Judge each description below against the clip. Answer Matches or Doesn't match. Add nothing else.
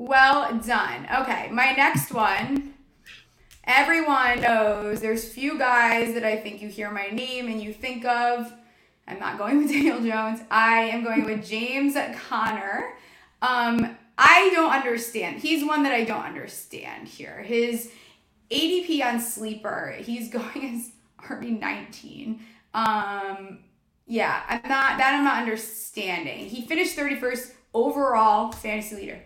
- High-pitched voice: Matches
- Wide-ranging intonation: Doesn't match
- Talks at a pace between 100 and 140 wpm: Matches